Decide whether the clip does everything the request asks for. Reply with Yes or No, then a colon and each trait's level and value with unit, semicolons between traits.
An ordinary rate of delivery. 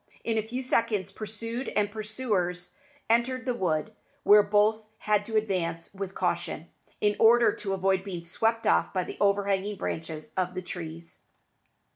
Yes: average, 155 wpm